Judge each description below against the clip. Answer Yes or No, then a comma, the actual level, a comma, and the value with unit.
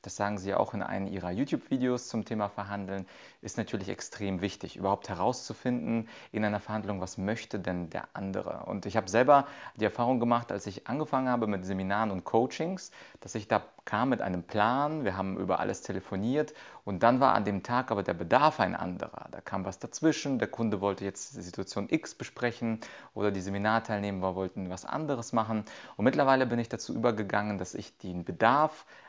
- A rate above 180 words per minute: Yes, fast, 190 wpm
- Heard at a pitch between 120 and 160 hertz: No, low, 105 Hz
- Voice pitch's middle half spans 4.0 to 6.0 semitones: No, average, 3.6 semitones